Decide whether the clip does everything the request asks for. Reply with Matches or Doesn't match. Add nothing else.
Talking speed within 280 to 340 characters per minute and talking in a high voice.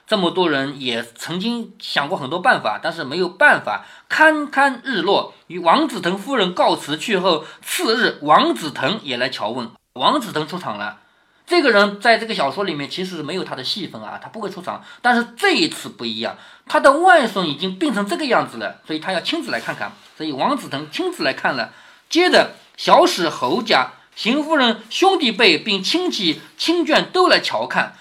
Matches